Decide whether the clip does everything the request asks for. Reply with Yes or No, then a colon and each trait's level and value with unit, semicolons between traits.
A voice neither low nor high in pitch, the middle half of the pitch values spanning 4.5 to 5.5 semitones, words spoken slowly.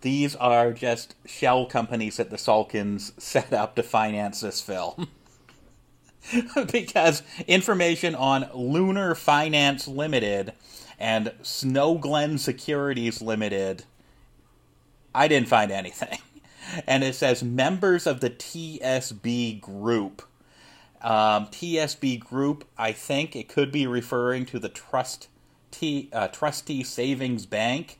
No: low, 125 Hz; average, 4.9 semitones; slow, 115 wpm